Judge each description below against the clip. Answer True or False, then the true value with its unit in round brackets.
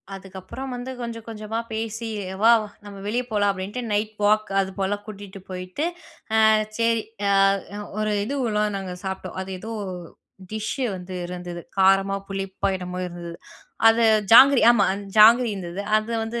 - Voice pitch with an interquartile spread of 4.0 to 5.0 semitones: False (3.1 semitones)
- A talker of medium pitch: False (210 Hz)